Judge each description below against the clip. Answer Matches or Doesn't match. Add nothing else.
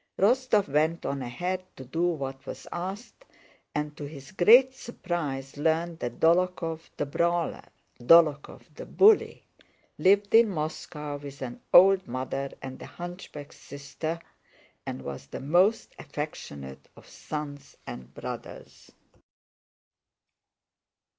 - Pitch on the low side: Doesn't match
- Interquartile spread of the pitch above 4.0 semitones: Matches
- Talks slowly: Matches